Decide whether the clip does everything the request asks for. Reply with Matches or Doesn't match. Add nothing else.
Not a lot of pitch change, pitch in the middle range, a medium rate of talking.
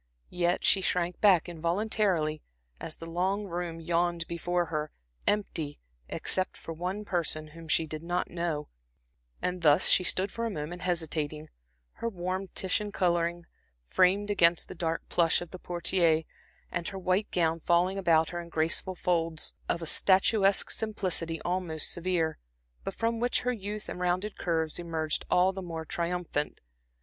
Matches